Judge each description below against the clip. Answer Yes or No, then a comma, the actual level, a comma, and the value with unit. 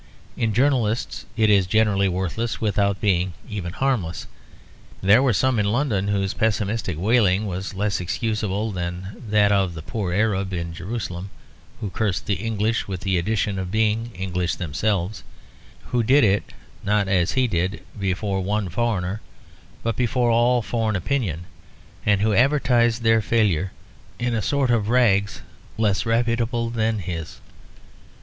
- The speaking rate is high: No, average, 145 wpm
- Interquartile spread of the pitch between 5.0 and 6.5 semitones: No, average, 3.3 semitones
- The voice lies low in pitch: Yes, low, 105 Hz